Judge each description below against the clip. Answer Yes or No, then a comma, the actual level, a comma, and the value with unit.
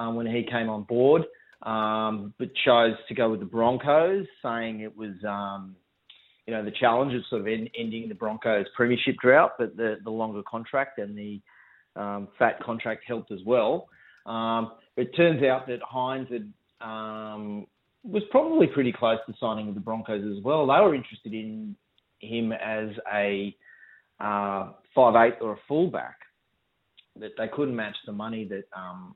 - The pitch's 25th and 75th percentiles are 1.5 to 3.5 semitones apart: Yes, average, 3.2 semitones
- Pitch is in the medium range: No, low, 110 Hz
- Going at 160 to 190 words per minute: Yes, average, 170 wpm